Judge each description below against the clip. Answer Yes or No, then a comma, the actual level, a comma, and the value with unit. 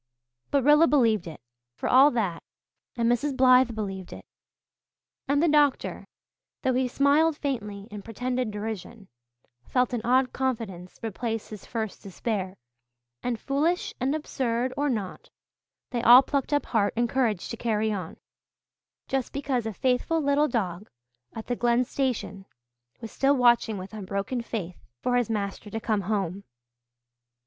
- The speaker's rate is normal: Yes, average, 150 wpm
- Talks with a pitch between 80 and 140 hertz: No, high, 235 Hz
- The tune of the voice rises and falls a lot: No, average, 4.0 semitones